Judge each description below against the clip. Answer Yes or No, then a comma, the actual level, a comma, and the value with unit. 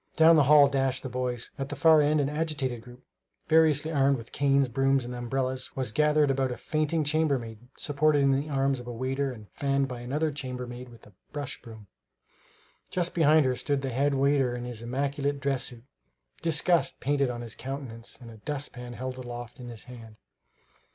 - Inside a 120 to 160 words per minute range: No, average, 190 wpm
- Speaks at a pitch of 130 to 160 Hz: Yes, low, 135 Hz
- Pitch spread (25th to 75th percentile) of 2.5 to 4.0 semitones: Yes, average, 2.9 semitones